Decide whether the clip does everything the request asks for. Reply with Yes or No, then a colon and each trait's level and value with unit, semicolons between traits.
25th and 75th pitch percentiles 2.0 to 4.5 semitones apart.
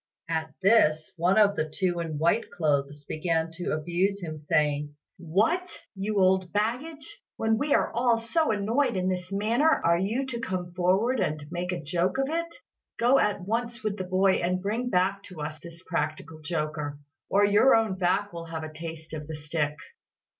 No: average, 5.3 semitones